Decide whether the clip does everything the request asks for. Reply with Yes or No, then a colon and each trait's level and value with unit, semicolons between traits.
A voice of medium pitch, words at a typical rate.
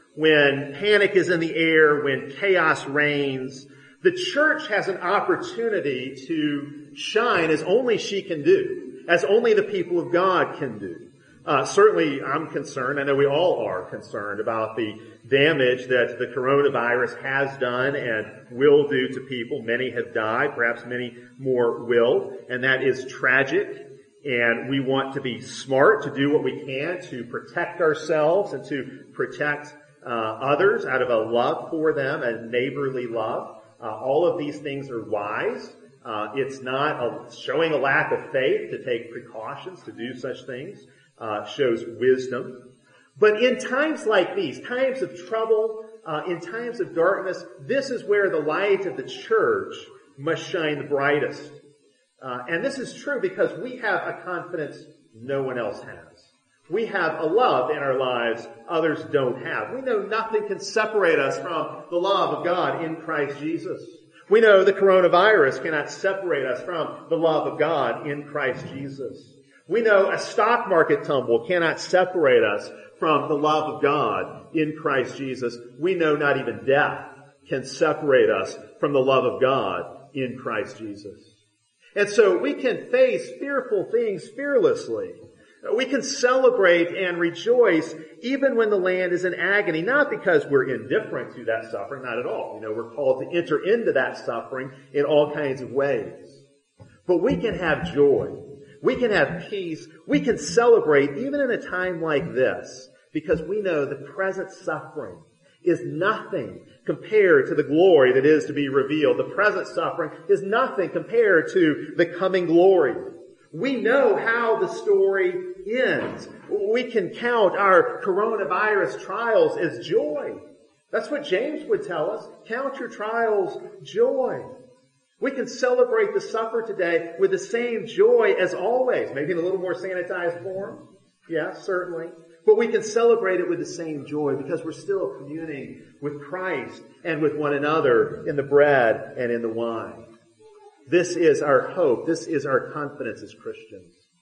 Yes: medium, 180 Hz; average, 165 wpm